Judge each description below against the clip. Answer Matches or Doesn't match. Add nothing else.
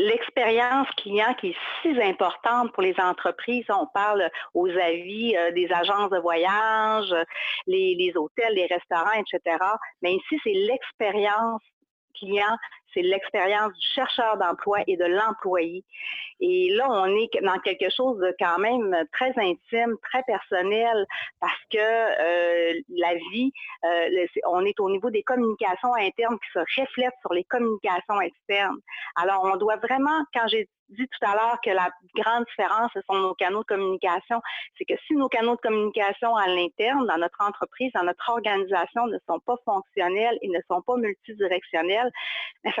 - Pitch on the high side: Matches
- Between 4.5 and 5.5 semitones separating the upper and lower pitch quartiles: Matches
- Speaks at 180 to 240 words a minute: Doesn't match